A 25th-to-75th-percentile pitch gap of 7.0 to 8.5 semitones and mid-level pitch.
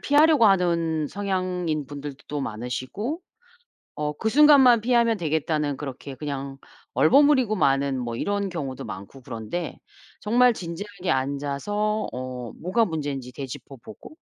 Yes: wide, 7.4 semitones; medium, 160 Hz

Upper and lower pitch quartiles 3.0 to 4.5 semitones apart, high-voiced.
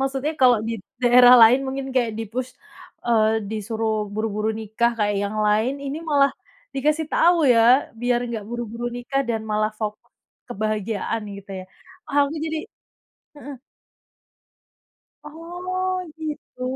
Yes: average, 4.2 semitones; high, 240 Hz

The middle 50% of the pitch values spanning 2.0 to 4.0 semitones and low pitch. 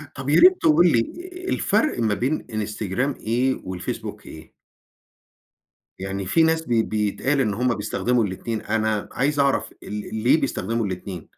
No: average, 4.8 semitones; low, 115 Hz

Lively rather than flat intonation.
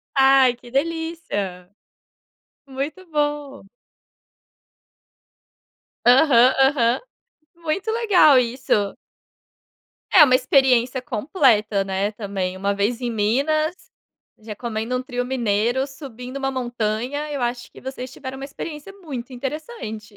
No: average, 4.1 semitones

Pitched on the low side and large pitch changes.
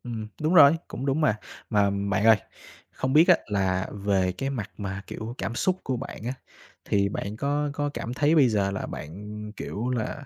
Yes: low, 115 Hz; wide, 5.8 semitones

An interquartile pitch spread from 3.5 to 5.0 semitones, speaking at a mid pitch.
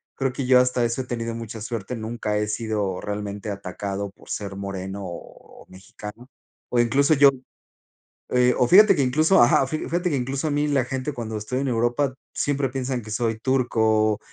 No: average, 4.0 semitones; low, 120 Hz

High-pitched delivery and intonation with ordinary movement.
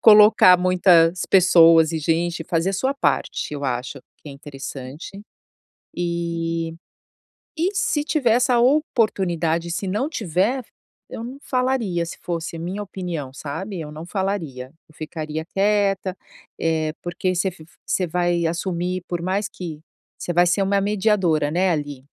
No: medium, 175 Hz; average, 3.4 semitones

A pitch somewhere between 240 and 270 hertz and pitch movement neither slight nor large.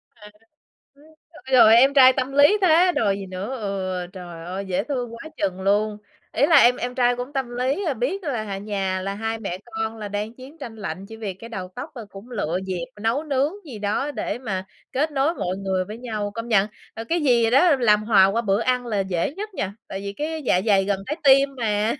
No: high, 225 Hz; average, 5.0 semitones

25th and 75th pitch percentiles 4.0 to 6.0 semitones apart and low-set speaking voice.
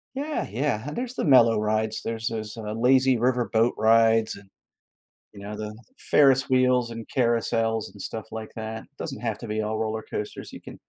No: average, 2.7 semitones; low, 115 Hz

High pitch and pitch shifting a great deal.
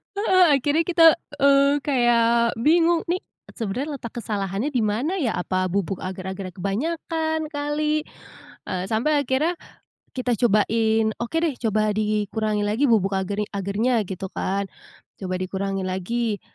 Yes: high, 230 Hz; wide, 6.5 semitones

